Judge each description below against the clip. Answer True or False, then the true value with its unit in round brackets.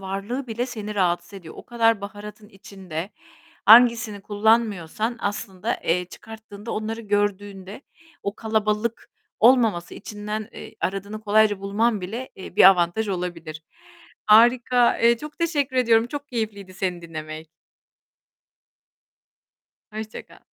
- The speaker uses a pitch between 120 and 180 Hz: False (210 Hz)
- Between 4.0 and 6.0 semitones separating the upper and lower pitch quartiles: False (2.9 semitones)